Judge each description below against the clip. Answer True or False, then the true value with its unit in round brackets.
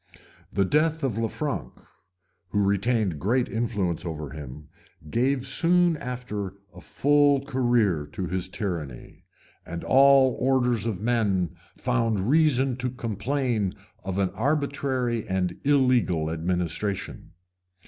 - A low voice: True (115 Hz)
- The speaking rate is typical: False (115 wpm)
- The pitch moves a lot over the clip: True (5.9 semitones)